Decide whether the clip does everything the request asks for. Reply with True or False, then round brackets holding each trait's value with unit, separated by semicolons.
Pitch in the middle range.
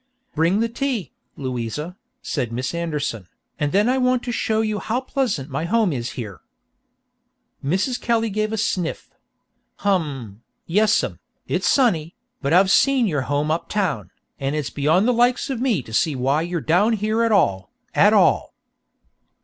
True (180 Hz)